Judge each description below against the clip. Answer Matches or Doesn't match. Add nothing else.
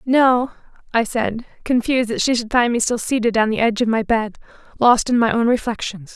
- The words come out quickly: Matches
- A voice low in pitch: Doesn't match